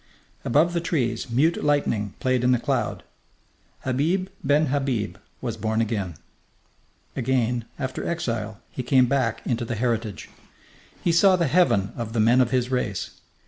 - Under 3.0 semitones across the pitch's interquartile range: No, average, 4.1 semitones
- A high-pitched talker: No, low, 125 Hz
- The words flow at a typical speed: Yes, average, 150 wpm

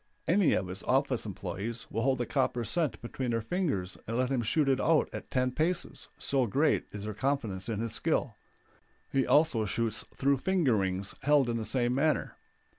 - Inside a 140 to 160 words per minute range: No, average, 190 wpm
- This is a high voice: No, low, 125 Hz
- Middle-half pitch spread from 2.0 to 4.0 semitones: No, average, 4.4 semitones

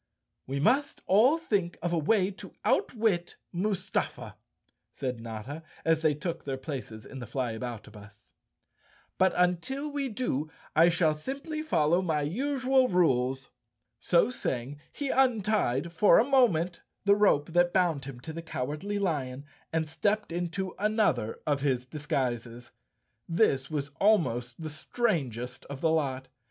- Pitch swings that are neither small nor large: No, wide, 7.3 semitones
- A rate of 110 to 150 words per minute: Yes, average, 145 wpm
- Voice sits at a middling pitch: Yes, medium, 165 Hz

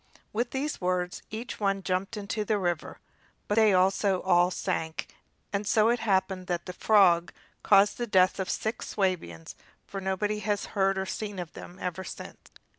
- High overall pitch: Yes, high, 195 Hz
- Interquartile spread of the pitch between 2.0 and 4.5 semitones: Yes, narrow, 2.4 semitones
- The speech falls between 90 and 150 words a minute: No, average, 175 wpm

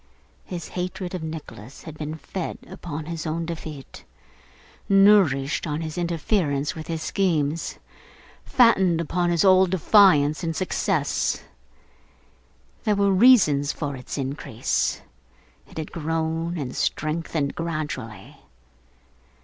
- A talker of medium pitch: Yes, medium, 160 Hz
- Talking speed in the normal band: No, slow, 115 wpm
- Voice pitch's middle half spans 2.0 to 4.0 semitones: Yes, average, 3.3 semitones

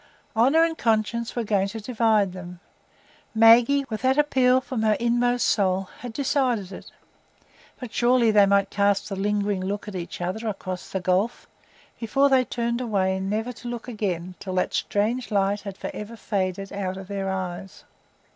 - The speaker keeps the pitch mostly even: No, average, 3.7 semitones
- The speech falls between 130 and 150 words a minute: No, average, 170 wpm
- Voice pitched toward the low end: No, high, 210 Hz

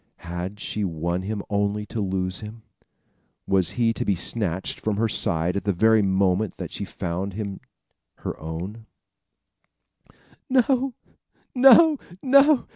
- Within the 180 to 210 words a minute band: No, slow, 135 wpm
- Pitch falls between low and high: No, low, 100 Hz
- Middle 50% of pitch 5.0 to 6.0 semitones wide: No, average, 3.6 semitones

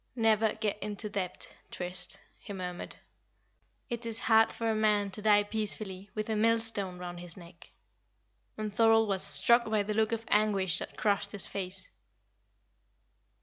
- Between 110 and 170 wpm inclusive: Yes, average, 155 wpm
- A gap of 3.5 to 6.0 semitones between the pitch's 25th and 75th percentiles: No, narrow, 2.5 semitones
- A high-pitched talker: Yes, high, 210 Hz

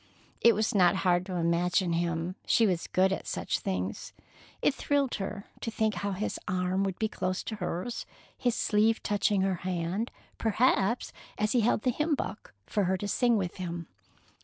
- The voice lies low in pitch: No, high, 195 Hz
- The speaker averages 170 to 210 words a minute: Yes, average, 185 wpm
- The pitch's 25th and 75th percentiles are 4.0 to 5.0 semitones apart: No, average, 3.6 semitones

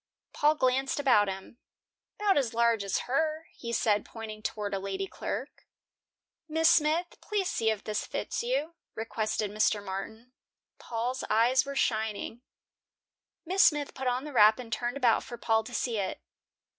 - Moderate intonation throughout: Yes, average, 4.7 semitones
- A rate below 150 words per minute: No, average, 160 wpm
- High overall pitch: Yes, high, 235 Hz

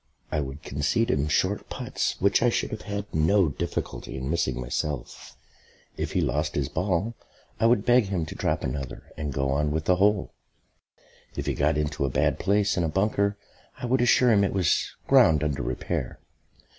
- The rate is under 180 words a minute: No, average, 190 wpm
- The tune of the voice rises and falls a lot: Yes, wide, 5.8 semitones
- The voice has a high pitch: No, very low, 85 Hz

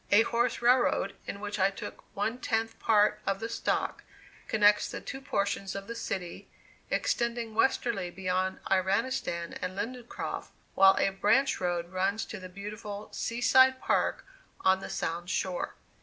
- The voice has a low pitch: No, high, 205 Hz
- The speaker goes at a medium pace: Yes, average, 155 wpm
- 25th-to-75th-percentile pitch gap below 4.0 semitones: Yes, average, 3.6 semitones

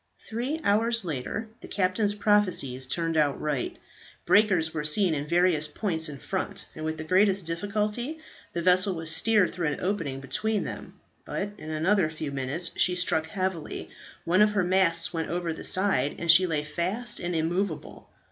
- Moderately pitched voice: Yes, medium, 175 Hz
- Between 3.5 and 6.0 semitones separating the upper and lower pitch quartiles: Yes, average, 4.3 semitones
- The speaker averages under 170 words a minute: No, average, 175 wpm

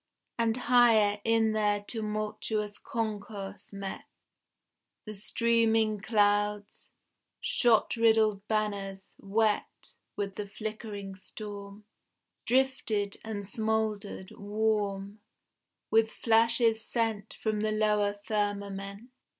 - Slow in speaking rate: Yes, slow, 90 wpm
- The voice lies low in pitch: No, high, 215 Hz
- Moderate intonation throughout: No, narrow, 1.5 semitones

